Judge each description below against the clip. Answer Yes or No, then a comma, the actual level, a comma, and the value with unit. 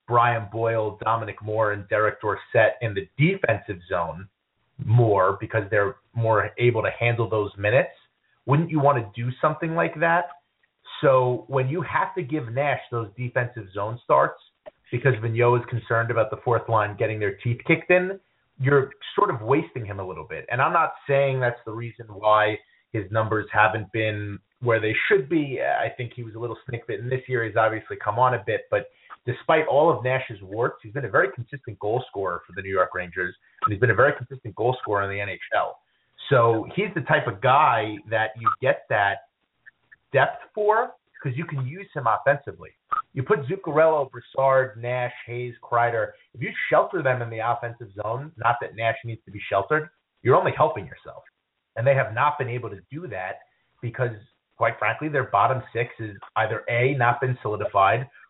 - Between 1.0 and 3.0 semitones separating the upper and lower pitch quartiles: No, average, 3.9 semitones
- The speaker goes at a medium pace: Yes, average, 190 wpm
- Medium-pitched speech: No, low, 120 Hz